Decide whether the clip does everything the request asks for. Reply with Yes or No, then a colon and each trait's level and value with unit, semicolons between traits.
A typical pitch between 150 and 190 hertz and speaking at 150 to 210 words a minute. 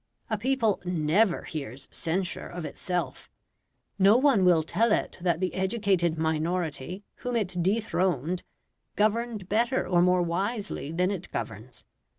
No: medium, 185 Hz; slow, 135 wpm